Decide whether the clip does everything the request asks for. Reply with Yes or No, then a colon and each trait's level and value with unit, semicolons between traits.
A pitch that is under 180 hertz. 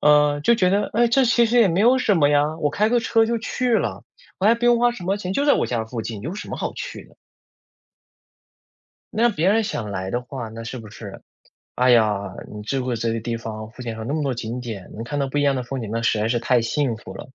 Yes: medium, 140 Hz